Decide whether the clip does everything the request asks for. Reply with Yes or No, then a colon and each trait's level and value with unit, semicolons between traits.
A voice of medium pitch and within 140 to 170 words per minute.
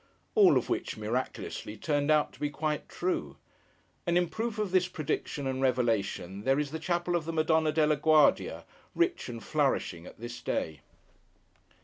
Yes: medium, 155 Hz; average, 165 wpm